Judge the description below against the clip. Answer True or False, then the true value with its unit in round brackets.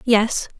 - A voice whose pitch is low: False (225 Hz)